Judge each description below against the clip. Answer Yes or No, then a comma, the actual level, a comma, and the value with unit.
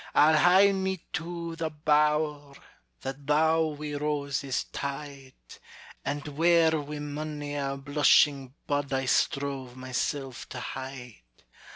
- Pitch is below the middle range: No, medium, 145 Hz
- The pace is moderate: No, slow, 115 wpm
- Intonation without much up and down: Yes, narrow, 2.1 semitones